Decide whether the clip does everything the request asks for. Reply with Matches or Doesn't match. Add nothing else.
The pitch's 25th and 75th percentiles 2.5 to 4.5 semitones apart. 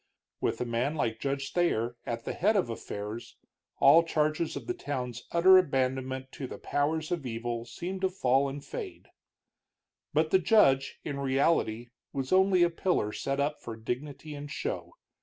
Doesn't match